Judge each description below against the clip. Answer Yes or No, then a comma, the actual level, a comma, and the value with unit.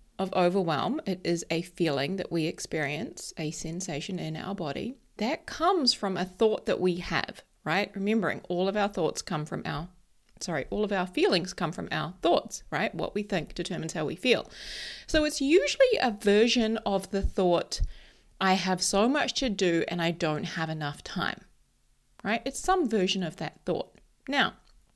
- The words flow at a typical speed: Yes, average, 185 wpm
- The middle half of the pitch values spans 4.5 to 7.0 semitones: No, average, 4.1 semitones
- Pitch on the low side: No, medium, 185 Hz